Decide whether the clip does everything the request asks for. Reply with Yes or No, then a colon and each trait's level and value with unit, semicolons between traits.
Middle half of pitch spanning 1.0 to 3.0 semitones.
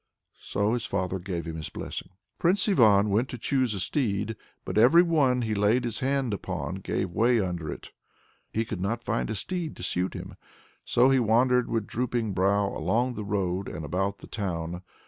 No: average, 4.5 semitones